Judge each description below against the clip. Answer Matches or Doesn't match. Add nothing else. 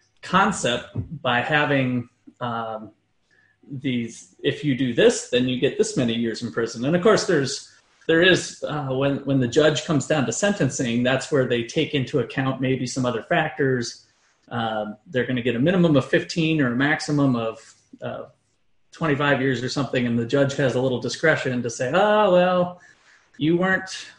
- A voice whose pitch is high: Doesn't match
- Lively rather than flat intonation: Doesn't match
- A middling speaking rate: Matches